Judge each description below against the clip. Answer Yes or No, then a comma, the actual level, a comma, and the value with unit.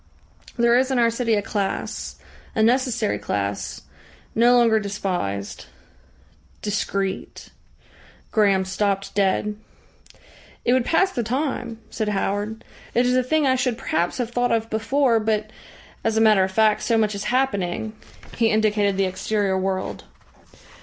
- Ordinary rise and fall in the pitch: Yes, average, 3.4 semitones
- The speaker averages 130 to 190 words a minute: Yes, average, 150 wpm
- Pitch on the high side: Yes, high, 220 Hz